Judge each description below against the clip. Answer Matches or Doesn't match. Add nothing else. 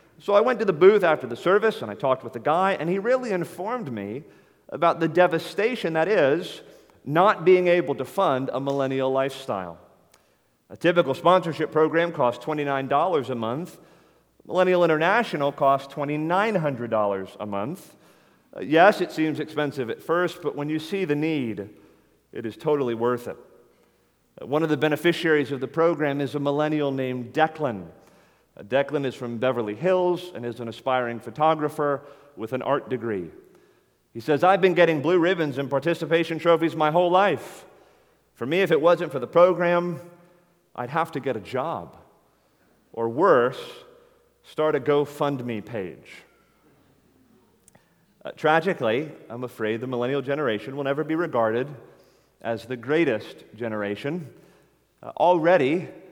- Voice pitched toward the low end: Doesn't match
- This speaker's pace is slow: Doesn't match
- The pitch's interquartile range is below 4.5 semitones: Doesn't match